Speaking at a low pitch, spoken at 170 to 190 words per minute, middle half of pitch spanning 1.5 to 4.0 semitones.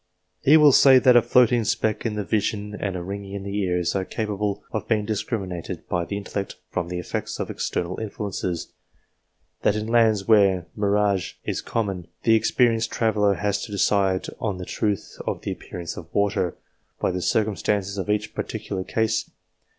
Yes: low, 100 Hz; average, 180 wpm; narrow, 2.6 semitones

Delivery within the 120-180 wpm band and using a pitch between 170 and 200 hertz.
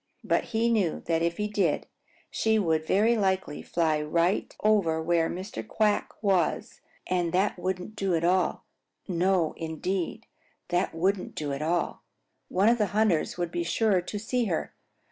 Yes: average, 165 wpm; medium, 185 Hz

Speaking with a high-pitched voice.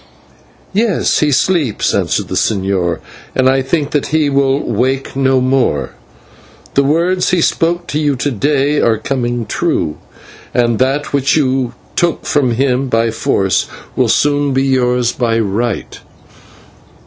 No: low, 135 Hz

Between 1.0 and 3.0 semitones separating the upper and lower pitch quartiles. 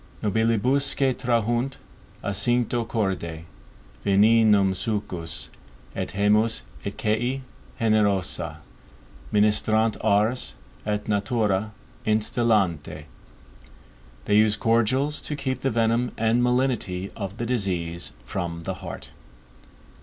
No: average, 3.4 semitones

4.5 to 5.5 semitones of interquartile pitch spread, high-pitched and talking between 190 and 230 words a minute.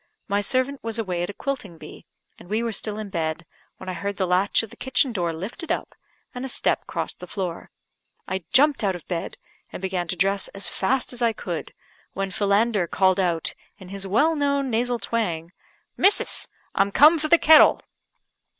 Yes: average, 5.1 semitones; high, 200 Hz; average, 195 wpm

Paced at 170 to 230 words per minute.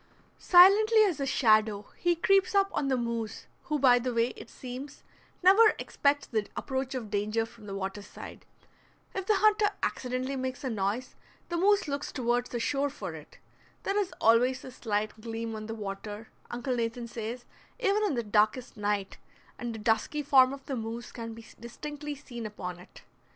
Yes: average, 180 wpm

